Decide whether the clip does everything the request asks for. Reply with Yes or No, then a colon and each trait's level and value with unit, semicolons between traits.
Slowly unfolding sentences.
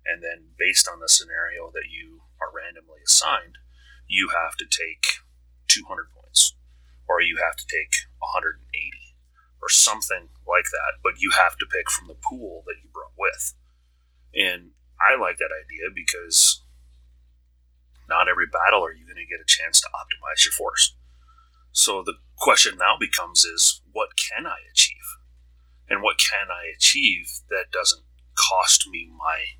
No: average, 160 wpm